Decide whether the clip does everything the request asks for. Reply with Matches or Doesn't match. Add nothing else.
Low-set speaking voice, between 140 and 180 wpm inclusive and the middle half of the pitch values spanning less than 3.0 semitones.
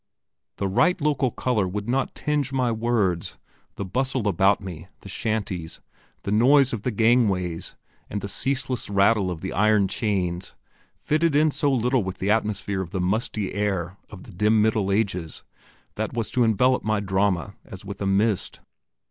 Doesn't match